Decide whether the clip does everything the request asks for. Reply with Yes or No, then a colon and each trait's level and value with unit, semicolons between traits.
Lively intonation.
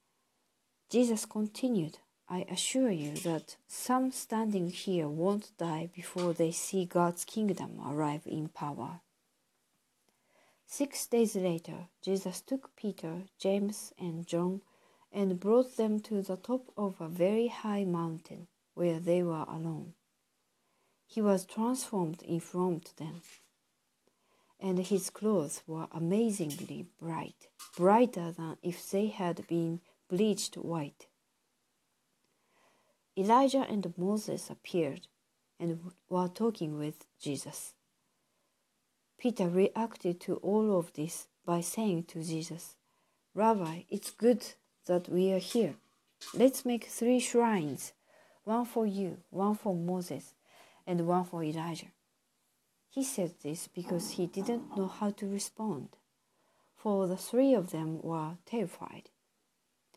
No: average, 4.1 semitones